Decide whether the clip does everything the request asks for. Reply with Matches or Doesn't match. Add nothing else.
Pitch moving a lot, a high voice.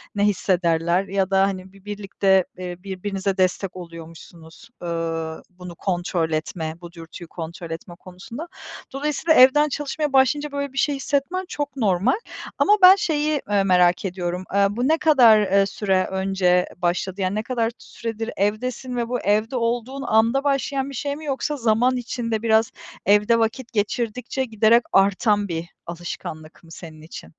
Matches